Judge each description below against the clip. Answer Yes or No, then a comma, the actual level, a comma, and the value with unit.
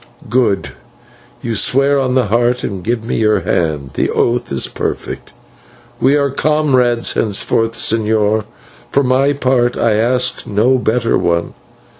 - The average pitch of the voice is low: Yes, low, 120 Hz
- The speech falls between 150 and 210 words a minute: No, average, 140 wpm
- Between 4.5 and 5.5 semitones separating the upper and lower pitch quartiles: No, average, 3.1 semitones